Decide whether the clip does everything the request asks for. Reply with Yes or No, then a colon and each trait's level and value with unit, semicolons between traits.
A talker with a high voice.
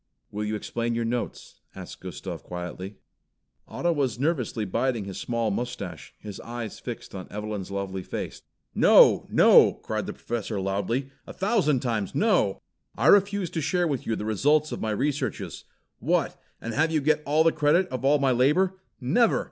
No: low, 125 Hz